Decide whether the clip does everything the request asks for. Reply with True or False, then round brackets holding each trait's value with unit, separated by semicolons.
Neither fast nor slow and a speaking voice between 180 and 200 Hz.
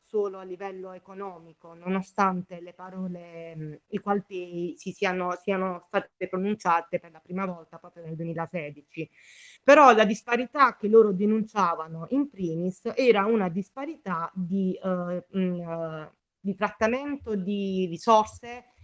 True (130 wpm; 185 Hz)